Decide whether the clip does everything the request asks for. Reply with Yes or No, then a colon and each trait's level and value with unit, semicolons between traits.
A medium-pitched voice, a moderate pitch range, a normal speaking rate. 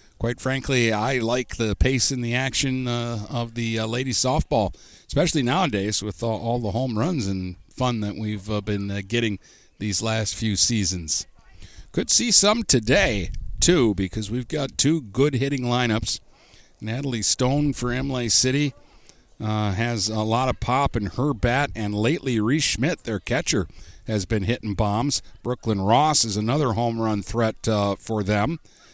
No: low, 115 Hz; average, 3.4 semitones; average, 170 wpm